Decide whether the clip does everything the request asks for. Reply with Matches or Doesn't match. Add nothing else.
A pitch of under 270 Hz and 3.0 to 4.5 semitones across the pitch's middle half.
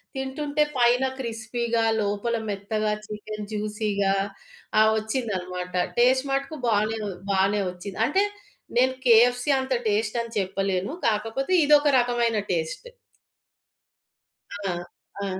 Matches